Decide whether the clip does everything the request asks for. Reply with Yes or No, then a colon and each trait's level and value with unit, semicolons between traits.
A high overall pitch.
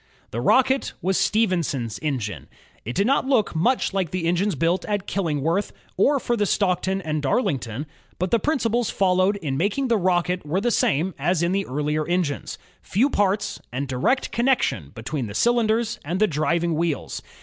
No: medium, 180 Hz